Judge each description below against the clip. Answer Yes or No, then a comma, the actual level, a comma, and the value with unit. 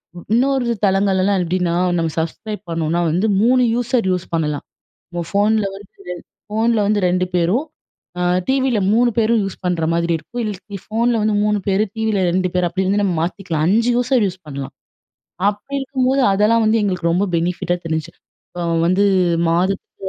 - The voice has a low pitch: No, high, 200 Hz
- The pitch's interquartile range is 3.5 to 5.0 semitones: Yes, average, 4.2 semitones